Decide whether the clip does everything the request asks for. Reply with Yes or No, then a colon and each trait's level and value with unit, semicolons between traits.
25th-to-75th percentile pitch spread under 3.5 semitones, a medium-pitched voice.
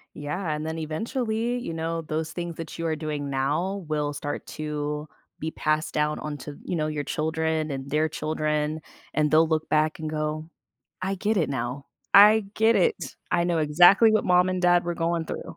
Yes: narrow, 2.5 semitones; medium, 155 Hz